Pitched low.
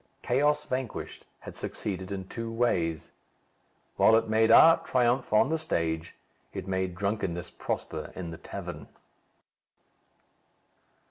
Yes: low, 105 Hz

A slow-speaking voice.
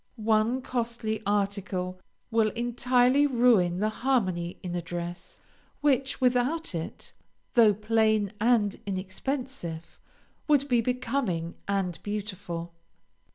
Yes: slow, 105 wpm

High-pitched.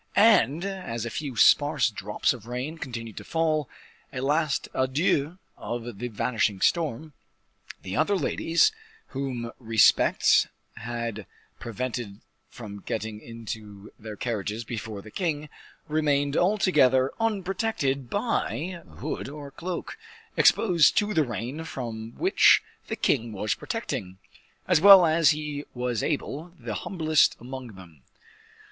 No: low, 130 Hz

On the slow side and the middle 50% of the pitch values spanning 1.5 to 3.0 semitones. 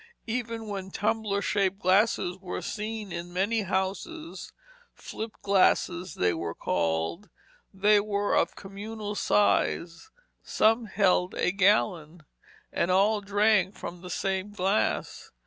Yes: slow, 120 wpm; narrow, 2.6 semitones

